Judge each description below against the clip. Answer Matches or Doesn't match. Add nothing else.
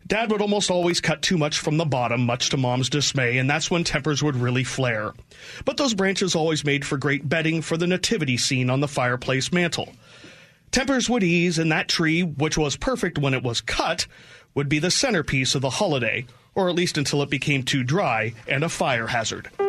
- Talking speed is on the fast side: Matches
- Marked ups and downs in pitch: Doesn't match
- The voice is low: Doesn't match